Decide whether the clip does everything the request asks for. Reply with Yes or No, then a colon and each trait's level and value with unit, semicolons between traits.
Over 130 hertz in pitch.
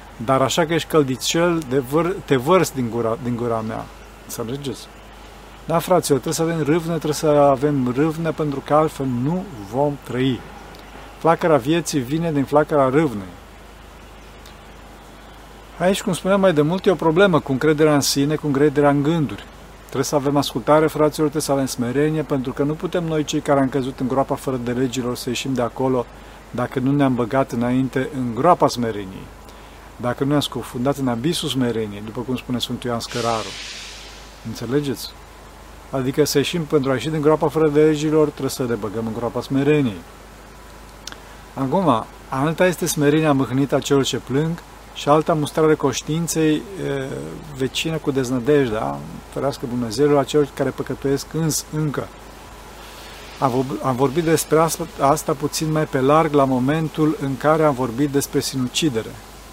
Yes: medium, 140 Hz